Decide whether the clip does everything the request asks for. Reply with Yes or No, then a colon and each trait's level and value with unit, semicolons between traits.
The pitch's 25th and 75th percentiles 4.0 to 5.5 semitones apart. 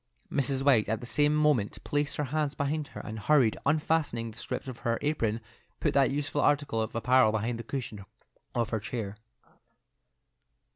Yes: average, 4.5 semitones